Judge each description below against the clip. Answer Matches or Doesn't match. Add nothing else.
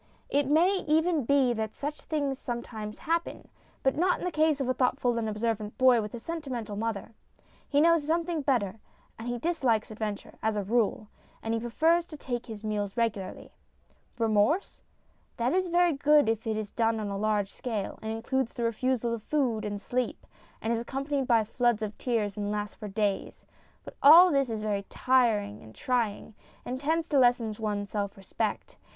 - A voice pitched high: Matches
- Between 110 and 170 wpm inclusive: Doesn't match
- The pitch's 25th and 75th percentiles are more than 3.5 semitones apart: Matches